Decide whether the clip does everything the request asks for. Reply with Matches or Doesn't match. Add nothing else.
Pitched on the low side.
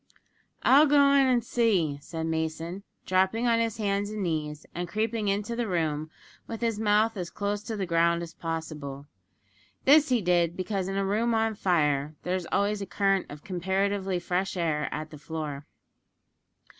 Doesn't match